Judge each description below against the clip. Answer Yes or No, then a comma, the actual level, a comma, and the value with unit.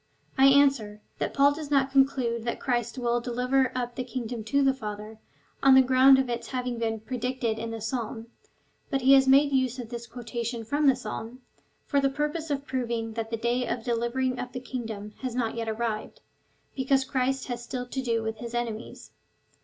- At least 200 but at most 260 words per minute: Yes, fast, 205 wpm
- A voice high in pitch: Yes, high, 245 Hz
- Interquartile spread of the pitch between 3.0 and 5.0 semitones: No, narrow, 2.5 semitones